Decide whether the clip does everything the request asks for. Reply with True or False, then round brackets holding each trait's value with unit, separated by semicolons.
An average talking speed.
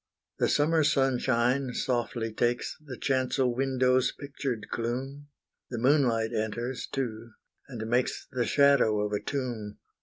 False (125 wpm)